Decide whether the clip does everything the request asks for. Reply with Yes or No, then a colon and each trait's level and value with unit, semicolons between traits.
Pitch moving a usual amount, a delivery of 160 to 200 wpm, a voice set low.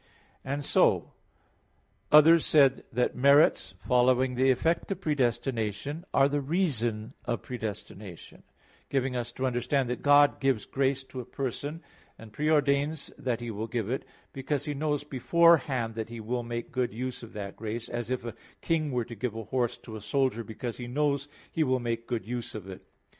Yes: average, 3.5 semitones; average, 180 wpm; low, 125 Hz